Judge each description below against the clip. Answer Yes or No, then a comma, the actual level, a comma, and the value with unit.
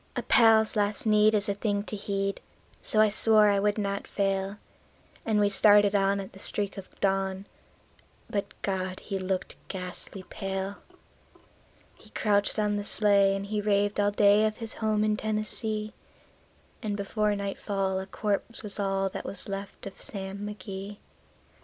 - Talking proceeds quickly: No, average, 165 wpm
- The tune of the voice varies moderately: No, narrow, 1.3 semitones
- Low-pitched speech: No, high, 205 Hz